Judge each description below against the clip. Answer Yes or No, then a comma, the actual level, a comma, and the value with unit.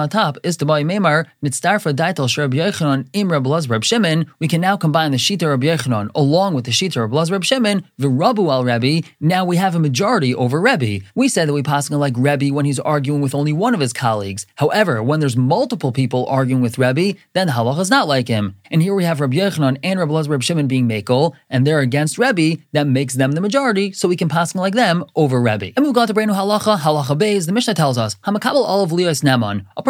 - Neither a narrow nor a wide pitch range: No, wide, 5.8 semitones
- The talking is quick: Yes, fast, 225 wpm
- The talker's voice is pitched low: No, medium, 150 Hz